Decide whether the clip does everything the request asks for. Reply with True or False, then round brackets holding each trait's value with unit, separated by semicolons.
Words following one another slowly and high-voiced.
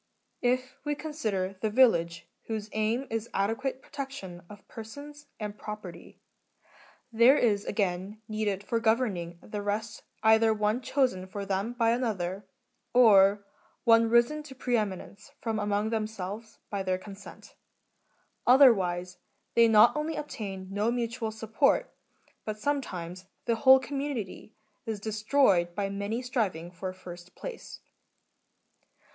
True (130 wpm; 215 Hz)